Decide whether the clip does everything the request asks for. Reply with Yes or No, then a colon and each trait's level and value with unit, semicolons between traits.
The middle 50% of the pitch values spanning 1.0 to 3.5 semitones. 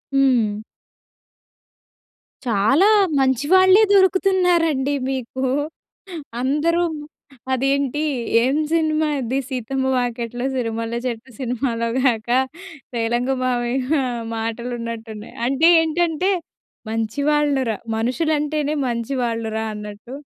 No: average, 4.3 semitones